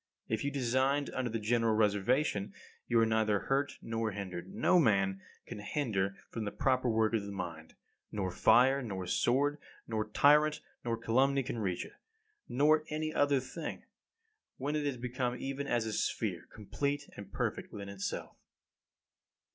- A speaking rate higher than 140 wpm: Yes, average, 155 wpm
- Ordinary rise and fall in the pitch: Yes, average, 5.0 semitones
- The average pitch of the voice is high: No, low, 115 Hz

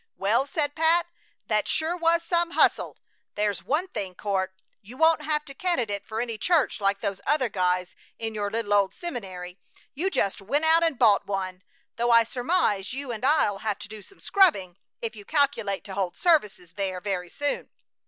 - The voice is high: Yes, high, 225 Hz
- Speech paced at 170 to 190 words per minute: Yes, average, 185 wpm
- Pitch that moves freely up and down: Yes, wide, 7.4 semitones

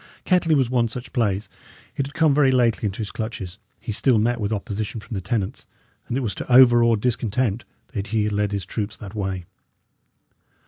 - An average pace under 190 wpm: No, average, 195 wpm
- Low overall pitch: Yes, low, 115 Hz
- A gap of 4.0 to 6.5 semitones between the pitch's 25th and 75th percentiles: No, average, 3.5 semitones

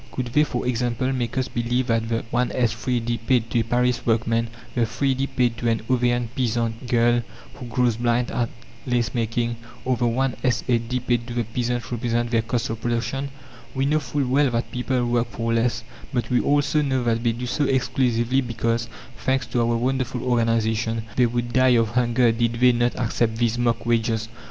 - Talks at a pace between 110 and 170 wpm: No, average, 195 wpm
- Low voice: Yes, low, 120 Hz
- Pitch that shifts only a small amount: Yes, narrow, 1.4 semitones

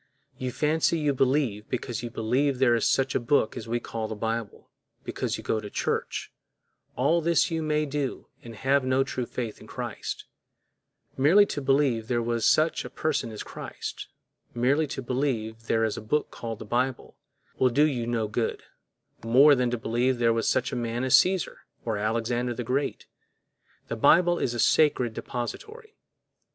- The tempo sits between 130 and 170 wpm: No, average, 180 wpm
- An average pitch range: Yes, average, 3.7 semitones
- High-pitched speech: No, low, 125 Hz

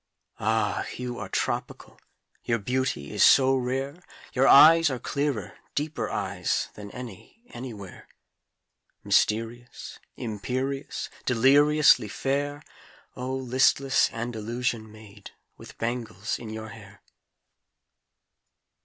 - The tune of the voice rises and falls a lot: No, average, 3.5 semitones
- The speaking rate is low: Yes, slow, 100 wpm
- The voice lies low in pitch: Yes, low, 125 Hz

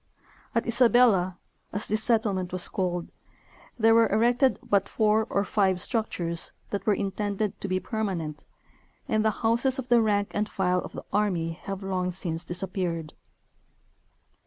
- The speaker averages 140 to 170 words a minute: Yes, average, 150 wpm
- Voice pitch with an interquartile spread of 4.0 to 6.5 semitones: No, average, 3.4 semitones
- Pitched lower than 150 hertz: No, high, 200 Hz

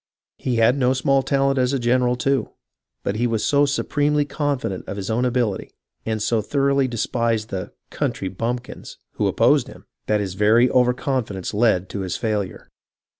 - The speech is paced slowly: No, average, 180 wpm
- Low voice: Yes, low, 120 Hz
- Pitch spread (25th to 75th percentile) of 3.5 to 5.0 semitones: Yes, average, 3.9 semitones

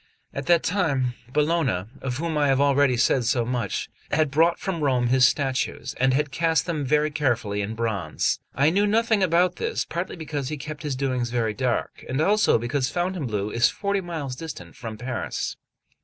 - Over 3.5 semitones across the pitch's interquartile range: Yes, average, 4.8 semitones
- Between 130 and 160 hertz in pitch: Yes, medium, 140 Hz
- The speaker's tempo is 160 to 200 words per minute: Yes, average, 185 wpm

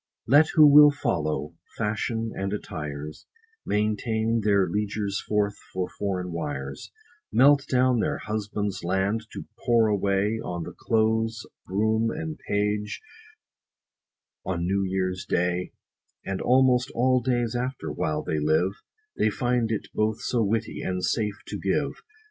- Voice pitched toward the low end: Yes, low, 105 Hz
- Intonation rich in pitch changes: No, average, 3.6 semitones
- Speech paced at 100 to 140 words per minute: Yes, slow, 135 wpm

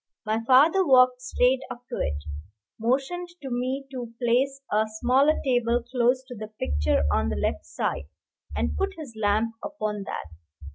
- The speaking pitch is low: No, high, 245 Hz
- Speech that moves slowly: No, average, 160 wpm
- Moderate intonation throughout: Yes, average, 3.7 semitones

